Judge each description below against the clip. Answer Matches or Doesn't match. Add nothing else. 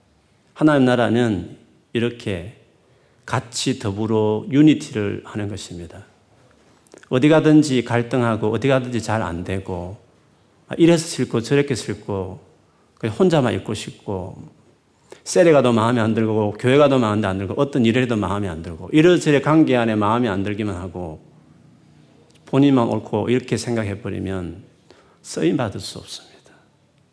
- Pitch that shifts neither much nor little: Matches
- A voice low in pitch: Matches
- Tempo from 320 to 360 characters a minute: Doesn't match